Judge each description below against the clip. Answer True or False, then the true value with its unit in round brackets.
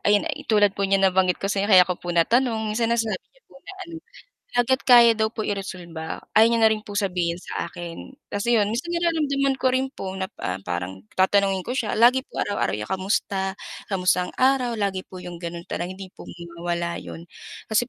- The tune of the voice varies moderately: True (4.4 semitones)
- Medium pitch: False (200 Hz)